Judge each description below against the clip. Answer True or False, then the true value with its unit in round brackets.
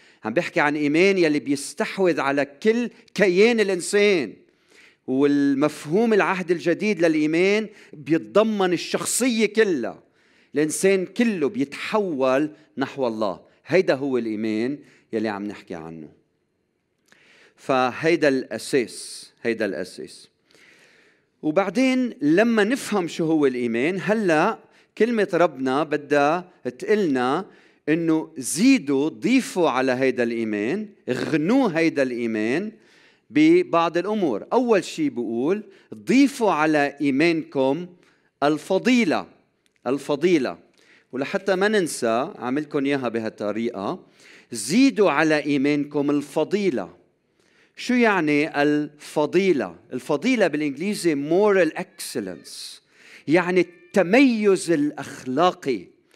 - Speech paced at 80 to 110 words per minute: True (90 wpm)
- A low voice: False (165 Hz)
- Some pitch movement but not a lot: False (6.3 semitones)